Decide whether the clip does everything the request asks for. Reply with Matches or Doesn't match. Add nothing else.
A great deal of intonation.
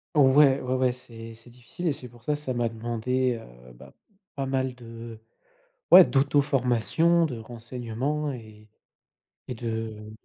Doesn't match